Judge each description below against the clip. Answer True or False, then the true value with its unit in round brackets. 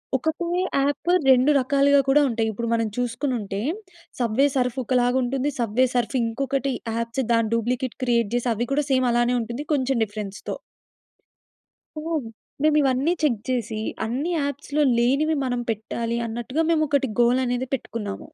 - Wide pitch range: False (3.0 semitones)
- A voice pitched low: False (250 Hz)